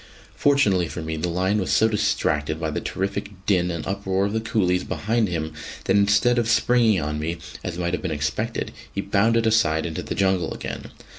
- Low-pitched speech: Yes, very low, 95 Hz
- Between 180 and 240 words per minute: Yes, average, 200 wpm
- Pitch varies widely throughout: No, average, 4.1 semitones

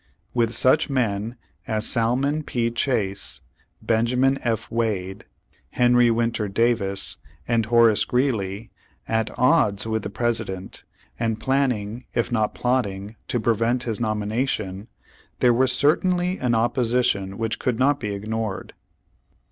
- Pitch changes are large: No, average, 2.7 semitones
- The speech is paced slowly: Yes, slow, 125 wpm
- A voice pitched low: Yes, low, 115 Hz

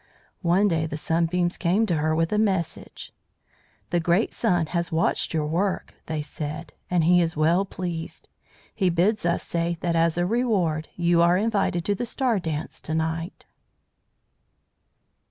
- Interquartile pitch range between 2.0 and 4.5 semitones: Yes, narrow, 2.5 semitones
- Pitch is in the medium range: Yes, medium, 170 Hz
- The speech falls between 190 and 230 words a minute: No, average, 160 wpm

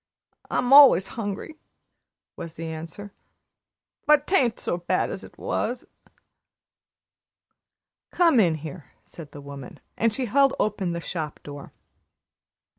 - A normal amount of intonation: No, wide, 8.0 semitones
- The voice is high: Yes, high, 195 Hz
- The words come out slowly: Yes, slow, 120 wpm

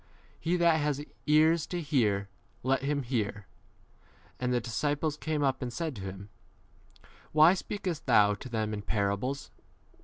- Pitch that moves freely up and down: Yes, wide, 6.3 semitones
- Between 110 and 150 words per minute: No, average, 160 wpm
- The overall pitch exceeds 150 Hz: No, low, 135 Hz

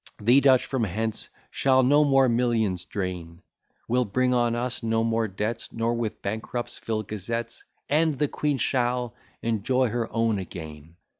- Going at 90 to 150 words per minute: No, average, 160 wpm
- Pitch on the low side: Yes, low, 115 Hz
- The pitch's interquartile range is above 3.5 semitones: No, average, 2.9 semitones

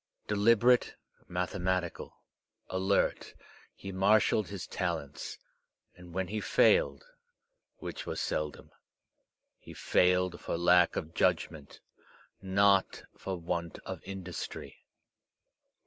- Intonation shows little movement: Yes, narrow, 2.2 semitones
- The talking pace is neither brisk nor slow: No, slow, 95 wpm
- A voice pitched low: Yes, very low, 95 Hz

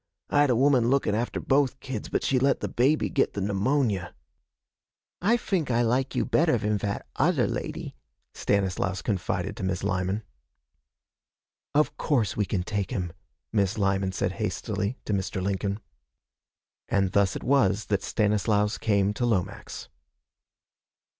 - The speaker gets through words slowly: No, average, 150 wpm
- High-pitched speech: No, low, 105 Hz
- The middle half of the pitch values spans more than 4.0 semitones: Yes, average, 4.6 semitones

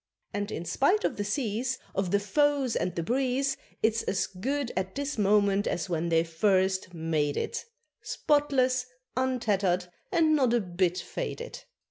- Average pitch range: No, wide, 6.4 semitones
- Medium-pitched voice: No, high, 210 Hz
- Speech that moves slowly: No, average, 155 wpm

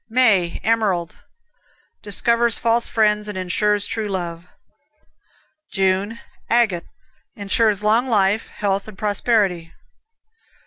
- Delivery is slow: Yes, slow, 95 wpm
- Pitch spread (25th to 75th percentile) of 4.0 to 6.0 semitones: No, average, 2.9 semitones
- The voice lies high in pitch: Yes, high, 210 Hz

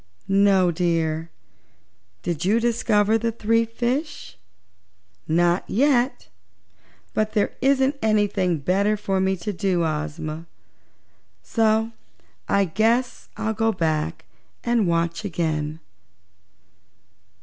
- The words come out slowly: Yes, slow, 100 wpm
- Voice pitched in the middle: No, high, 200 Hz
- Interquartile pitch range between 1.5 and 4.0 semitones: No, average, 5.0 semitones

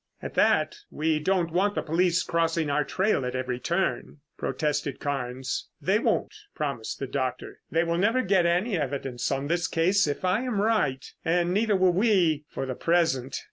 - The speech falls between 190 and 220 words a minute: No, average, 180 wpm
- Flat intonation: No, average, 5.1 semitones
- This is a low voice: No, medium, 165 Hz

